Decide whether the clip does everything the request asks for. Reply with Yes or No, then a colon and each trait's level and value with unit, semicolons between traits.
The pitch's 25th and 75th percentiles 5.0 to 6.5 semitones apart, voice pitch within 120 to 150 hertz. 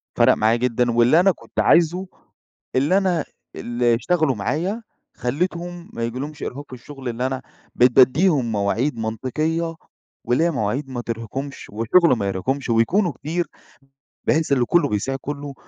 Yes: wide, 5.6 semitones; low, 135 Hz